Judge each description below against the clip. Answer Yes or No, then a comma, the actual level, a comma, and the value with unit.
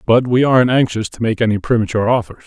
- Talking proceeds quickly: Yes, fast, 220 wpm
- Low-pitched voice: Yes, low, 115 Hz